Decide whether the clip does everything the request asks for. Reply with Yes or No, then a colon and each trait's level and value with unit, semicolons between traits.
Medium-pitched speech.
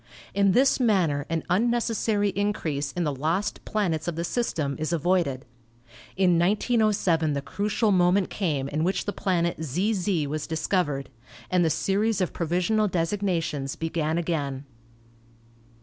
Yes: medium, 175 Hz